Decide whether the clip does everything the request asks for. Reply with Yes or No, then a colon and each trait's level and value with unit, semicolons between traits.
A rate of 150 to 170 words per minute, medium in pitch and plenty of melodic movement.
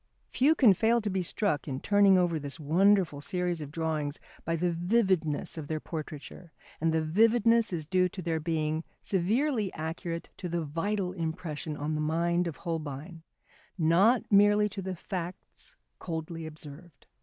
No: average, 160 wpm; medium, 170 Hz; average, 3.6 semitones